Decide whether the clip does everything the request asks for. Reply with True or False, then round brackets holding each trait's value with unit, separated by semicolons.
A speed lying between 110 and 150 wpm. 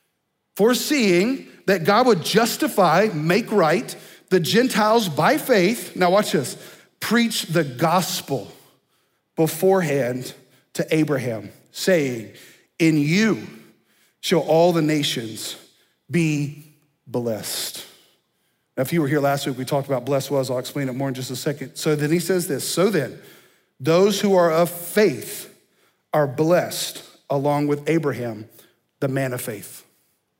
True (140 wpm)